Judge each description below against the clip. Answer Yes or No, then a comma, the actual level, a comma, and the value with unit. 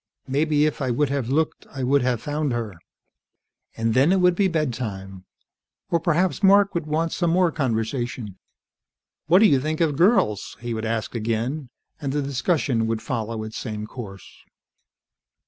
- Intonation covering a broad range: Yes, wide, 5.7 semitones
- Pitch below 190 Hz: Yes, low, 135 Hz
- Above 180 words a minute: No, average, 165 wpm